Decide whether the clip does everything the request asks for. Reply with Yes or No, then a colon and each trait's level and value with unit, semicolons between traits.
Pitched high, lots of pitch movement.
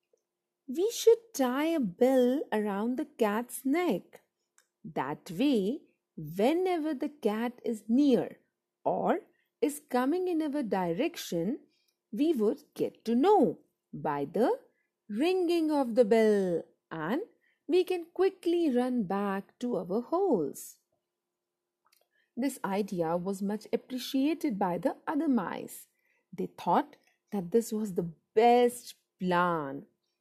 Yes: very high, 250 Hz; wide, 6.9 semitones